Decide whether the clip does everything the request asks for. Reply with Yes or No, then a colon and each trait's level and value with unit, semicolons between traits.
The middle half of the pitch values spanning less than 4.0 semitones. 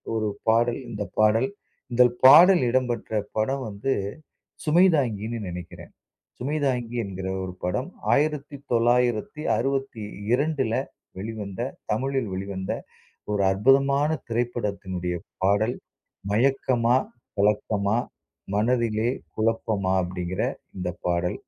No: average, 4.6 semitones